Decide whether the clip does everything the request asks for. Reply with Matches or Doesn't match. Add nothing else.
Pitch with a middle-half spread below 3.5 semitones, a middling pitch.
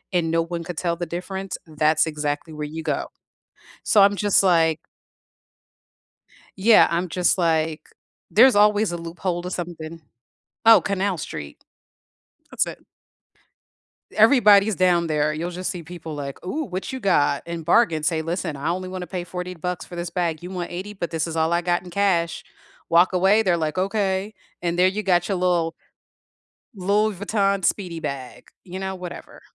Matches